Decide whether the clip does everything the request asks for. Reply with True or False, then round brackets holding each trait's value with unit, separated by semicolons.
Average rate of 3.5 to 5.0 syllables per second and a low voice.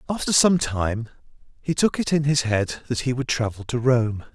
True (4.9 syllables/s; 130 Hz)